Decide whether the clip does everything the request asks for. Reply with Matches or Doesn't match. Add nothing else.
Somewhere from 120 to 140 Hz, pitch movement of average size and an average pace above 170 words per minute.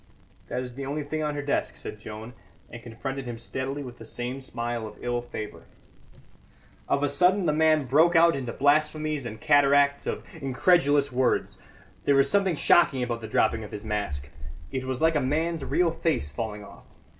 Matches